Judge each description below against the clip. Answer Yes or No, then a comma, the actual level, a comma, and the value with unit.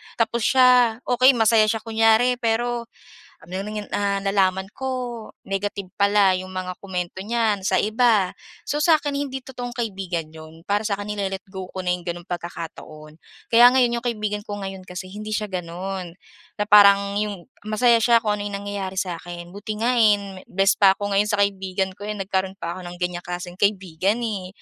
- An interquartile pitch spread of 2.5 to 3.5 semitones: Yes, average, 3.1 semitones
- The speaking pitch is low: No, high, 200 Hz